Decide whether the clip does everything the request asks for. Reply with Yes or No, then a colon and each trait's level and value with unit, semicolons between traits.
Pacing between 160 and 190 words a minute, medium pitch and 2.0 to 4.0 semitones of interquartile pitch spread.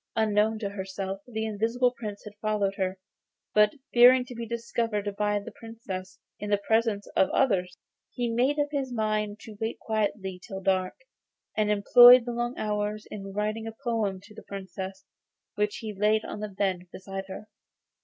No: average, 175 wpm; high, 210 Hz; narrow, 2.5 semitones